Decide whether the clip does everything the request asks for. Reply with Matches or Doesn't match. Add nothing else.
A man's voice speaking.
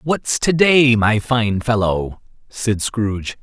Matches